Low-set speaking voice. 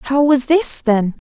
No: very high, 270 Hz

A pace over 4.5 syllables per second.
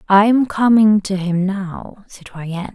No: 4.1 syllables/s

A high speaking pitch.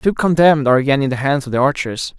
No: medium, 140 Hz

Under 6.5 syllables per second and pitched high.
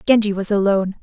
No: 7.1 syllables/s; high, 200 Hz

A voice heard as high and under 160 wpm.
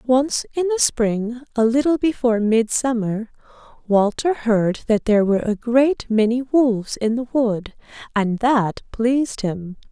Yes: high, 235 Hz; average, 145 wpm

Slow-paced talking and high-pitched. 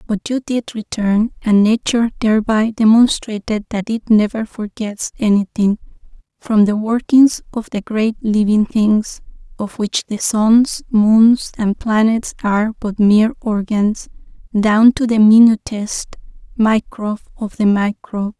Yes: slow, 130 wpm; high, 215 Hz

